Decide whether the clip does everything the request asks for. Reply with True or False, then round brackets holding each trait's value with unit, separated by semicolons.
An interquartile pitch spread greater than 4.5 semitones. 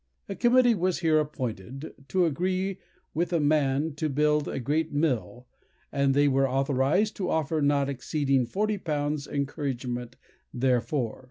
False (3.3 semitones)